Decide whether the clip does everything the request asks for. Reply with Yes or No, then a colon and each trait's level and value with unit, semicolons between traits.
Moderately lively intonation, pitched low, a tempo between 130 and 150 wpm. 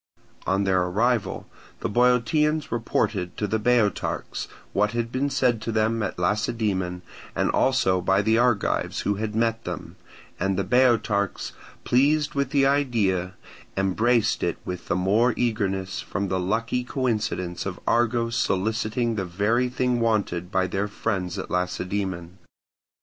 Yes: average, 4.2 semitones; low, 110 Hz; average, 145 wpm